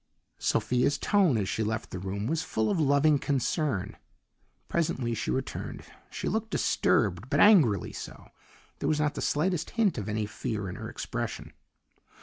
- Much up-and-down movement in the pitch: Yes, wide, 7.0 semitones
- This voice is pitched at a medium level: No, low, 130 Hz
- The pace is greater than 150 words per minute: Yes, average, 160 wpm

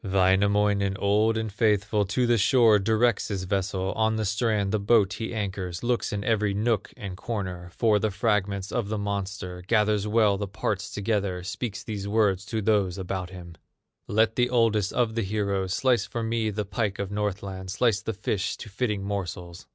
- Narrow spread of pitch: Yes, narrow, 2.3 semitones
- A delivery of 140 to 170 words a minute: No, average, 180 wpm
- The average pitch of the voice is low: Yes, low, 105 Hz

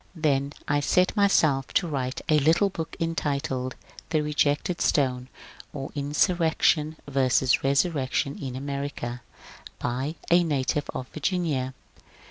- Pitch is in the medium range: Yes, medium, 145 Hz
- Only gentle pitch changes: No, average, 3.2 semitones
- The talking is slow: Yes, slow, 120 wpm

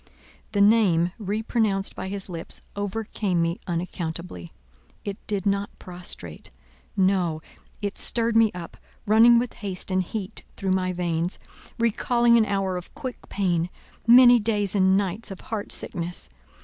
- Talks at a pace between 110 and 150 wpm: Yes, slow, 135 wpm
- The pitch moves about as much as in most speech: Yes, average, 3.4 semitones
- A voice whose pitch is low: No, high, 195 Hz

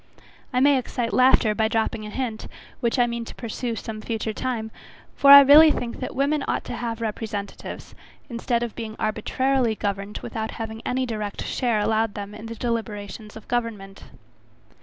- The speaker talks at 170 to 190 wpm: Yes, average, 175 wpm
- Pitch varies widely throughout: No, narrow, 2.4 semitones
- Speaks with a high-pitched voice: Yes, high, 230 Hz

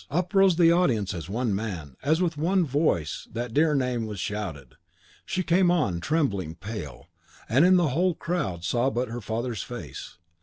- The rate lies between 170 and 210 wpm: Yes, average, 180 wpm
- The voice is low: Yes, low, 125 Hz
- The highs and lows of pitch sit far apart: Yes, wide, 8.7 semitones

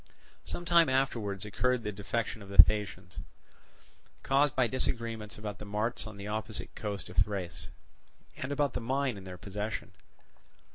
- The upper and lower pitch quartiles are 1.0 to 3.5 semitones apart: No, average, 4.1 semitones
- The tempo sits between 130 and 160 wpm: Yes, average, 155 wpm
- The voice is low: Yes, low, 105 Hz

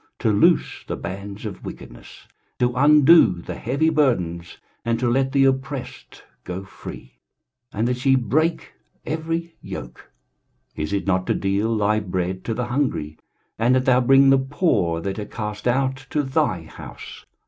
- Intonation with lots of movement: Yes, wide, 5.7 semitones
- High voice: No, low, 120 Hz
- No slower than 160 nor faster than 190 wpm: Yes, average, 165 wpm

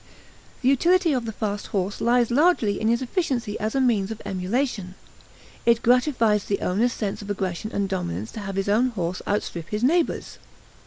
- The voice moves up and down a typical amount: Yes, average, 4.1 semitones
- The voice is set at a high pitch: Yes, high, 220 Hz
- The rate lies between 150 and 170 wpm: No, average, 180 wpm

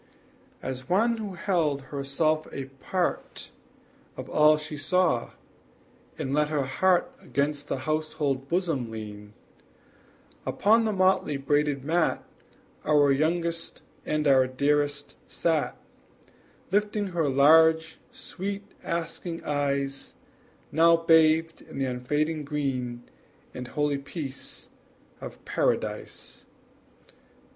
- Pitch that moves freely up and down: No, average, 3.4 semitones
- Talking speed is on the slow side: Yes, slow, 105 wpm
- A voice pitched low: No, medium, 150 Hz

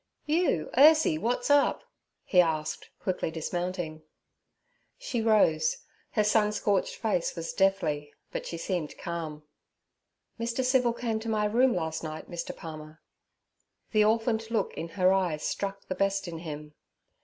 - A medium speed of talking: Yes, average, 145 wpm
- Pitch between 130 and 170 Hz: No, high, 195 Hz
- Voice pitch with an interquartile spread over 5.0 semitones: Yes, wide, 5.6 semitones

